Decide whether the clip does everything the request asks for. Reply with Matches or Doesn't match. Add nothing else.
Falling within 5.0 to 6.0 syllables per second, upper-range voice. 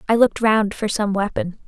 Matches